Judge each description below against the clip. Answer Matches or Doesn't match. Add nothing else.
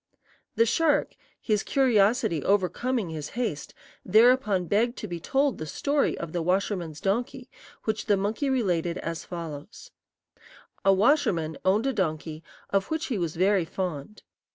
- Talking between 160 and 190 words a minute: Doesn't match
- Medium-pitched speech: Doesn't match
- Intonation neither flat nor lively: Doesn't match